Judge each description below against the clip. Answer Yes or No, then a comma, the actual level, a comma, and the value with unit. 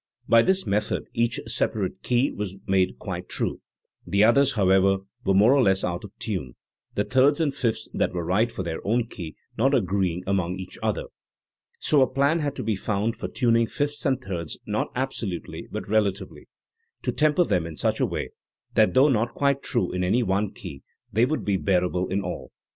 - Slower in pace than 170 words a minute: No, average, 200 wpm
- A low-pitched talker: Yes, low, 105 Hz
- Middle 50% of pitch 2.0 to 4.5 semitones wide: No, wide, 5.5 semitones